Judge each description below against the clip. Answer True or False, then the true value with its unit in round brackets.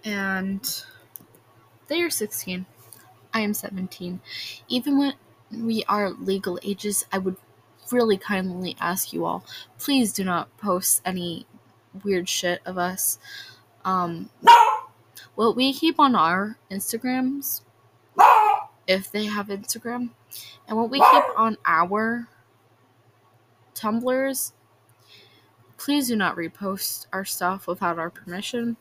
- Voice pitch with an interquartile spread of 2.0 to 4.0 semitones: False (4.9 semitones)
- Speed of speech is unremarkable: False (115 wpm)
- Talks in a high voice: True (195 Hz)